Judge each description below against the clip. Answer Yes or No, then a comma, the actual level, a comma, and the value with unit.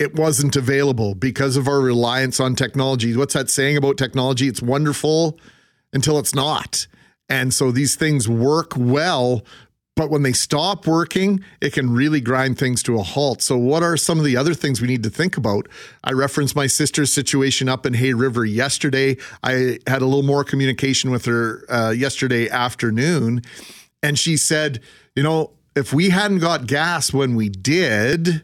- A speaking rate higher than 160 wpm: Yes, average, 180 wpm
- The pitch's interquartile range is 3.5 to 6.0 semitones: No, average, 2.8 semitones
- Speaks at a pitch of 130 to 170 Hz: Yes, low, 135 Hz